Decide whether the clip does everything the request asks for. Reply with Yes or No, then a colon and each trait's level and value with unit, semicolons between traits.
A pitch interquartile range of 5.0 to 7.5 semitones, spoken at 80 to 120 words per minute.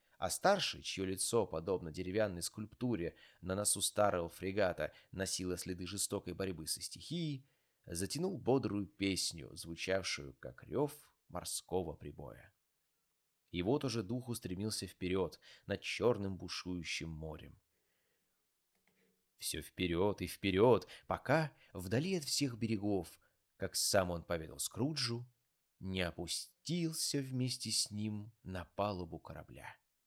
Yes: wide, 5.4 semitones; average, 115 wpm